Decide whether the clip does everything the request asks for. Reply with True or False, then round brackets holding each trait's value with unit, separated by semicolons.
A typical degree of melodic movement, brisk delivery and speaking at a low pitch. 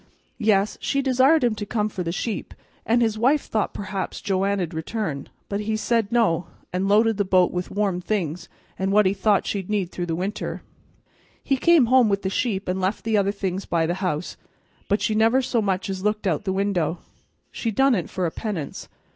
False (3.1 semitones; 210 wpm; 200 Hz)